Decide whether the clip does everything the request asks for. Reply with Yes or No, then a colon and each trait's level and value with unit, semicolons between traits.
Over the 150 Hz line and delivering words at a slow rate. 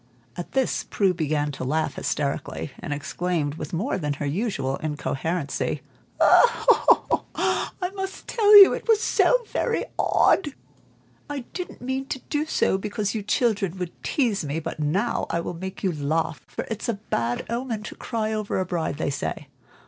No: high, 190 Hz; average, 170 wpm